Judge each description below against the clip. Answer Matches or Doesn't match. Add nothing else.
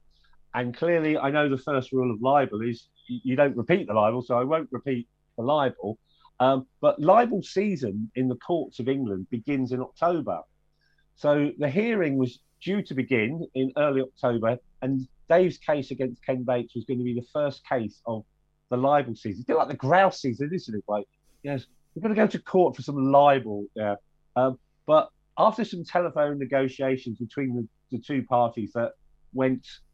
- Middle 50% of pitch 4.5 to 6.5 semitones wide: Doesn't match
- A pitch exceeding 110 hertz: Matches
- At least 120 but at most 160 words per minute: Doesn't match